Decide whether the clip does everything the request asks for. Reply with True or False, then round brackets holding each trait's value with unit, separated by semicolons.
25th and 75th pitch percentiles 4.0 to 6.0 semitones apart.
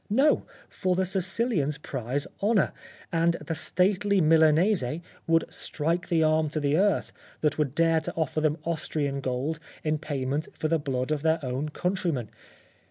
False (3.2 semitones)